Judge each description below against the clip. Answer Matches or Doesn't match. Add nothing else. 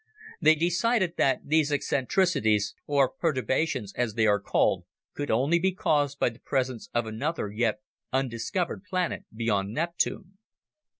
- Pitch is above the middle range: Doesn't match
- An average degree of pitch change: Doesn't match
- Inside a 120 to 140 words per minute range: Matches